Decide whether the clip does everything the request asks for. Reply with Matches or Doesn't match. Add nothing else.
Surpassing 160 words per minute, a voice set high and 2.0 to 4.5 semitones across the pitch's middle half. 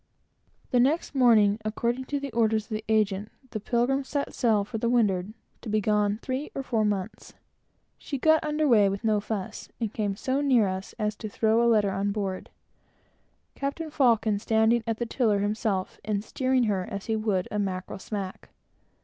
Matches